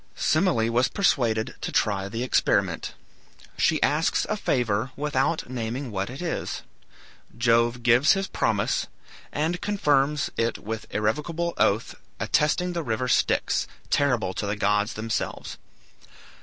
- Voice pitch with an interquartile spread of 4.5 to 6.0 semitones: Yes, average, 5.2 semitones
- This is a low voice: Yes, low, 125 Hz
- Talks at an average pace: No, slow, 130 wpm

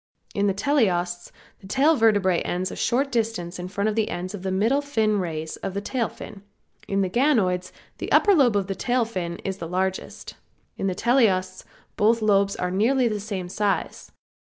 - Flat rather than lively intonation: No, average, 3.7 semitones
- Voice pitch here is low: No, high, 200 Hz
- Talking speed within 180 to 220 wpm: Yes, average, 190 wpm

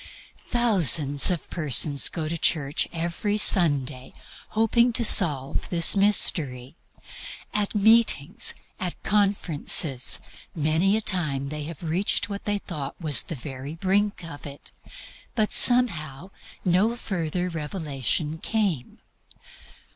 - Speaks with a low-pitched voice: No, medium, 170 Hz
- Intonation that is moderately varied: No, wide, 5.8 semitones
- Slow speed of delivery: Yes, slow, 115 wpm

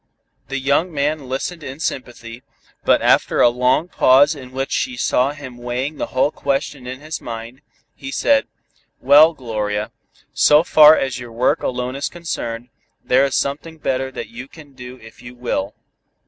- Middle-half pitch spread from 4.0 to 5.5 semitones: No, average, 3.0 semitones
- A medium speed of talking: Yes, average, 170 wpm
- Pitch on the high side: No, low, 130 Hz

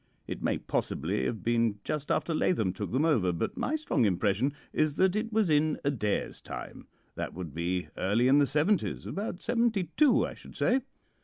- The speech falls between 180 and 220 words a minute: Yes, average, 185 wpm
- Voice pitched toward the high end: No, medium, 145 Hz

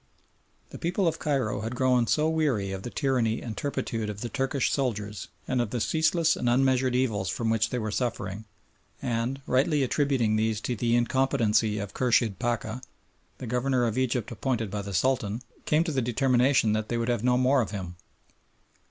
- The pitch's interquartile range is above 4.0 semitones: No, average, 3.4 semitones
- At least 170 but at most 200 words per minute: Yes, average, 185 wpm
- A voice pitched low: Yes, low, 120 Hz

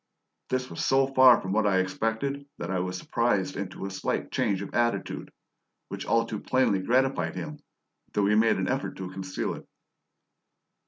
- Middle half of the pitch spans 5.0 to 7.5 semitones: Yes, average, 5.3 semitones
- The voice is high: No, low, 110 Hz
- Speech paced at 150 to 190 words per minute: Yes, average, 180 wpm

